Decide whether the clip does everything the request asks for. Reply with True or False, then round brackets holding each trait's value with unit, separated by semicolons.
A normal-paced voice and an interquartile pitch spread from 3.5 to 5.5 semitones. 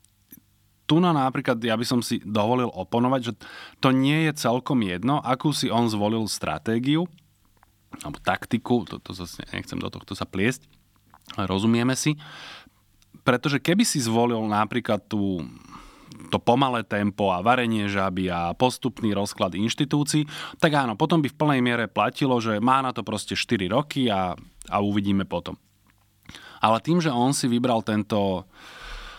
True (155 wpm; 4.2 semitones)